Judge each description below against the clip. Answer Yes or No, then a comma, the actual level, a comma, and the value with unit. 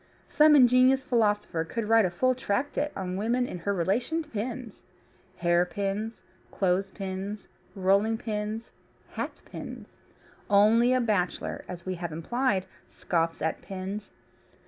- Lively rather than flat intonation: No, average, 4.3 semitones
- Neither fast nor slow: No, slow, 125 wpm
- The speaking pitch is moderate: No, high, 205 Hz